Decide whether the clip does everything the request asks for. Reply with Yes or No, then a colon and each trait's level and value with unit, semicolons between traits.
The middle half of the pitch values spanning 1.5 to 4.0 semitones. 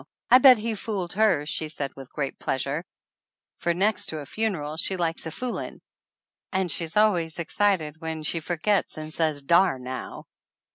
No: average, 4.7 semitones